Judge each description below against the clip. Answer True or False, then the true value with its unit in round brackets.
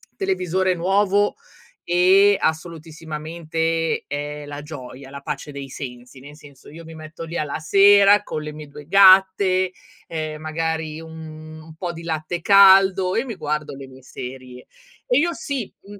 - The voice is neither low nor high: True (160 Hz)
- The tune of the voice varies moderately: True (4.0 semitones)